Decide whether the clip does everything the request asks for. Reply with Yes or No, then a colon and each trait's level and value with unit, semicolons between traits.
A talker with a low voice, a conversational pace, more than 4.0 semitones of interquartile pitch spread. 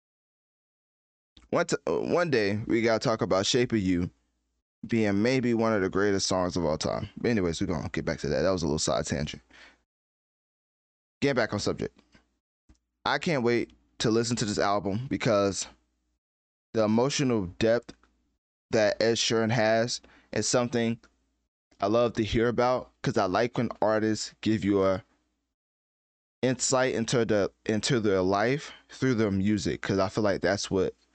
Yes: low, 105 Hz; average, 170 wpm; average, 4.8 semitones